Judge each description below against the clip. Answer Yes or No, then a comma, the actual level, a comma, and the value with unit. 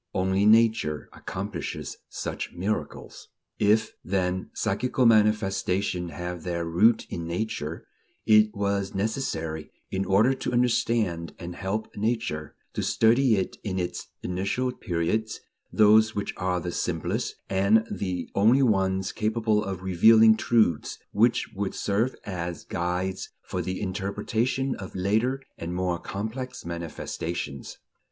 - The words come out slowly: Yes, slow, 125 wpm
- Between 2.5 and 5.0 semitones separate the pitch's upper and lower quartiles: Yes, average, 3.7 semitones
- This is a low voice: Yes, low, 100 Hz